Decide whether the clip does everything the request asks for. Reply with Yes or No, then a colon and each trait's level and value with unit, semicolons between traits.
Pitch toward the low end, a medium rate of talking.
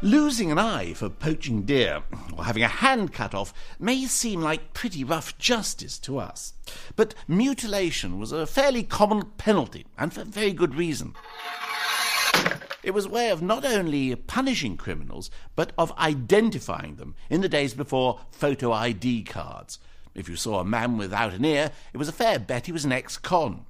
No: medium, 145 Hz; average, 175 wpm